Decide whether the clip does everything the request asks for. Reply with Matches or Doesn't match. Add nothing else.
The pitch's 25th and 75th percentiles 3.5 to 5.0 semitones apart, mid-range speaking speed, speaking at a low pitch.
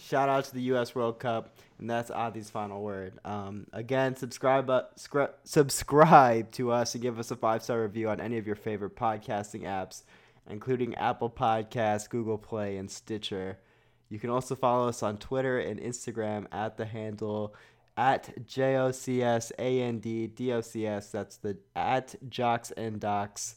Doesn't match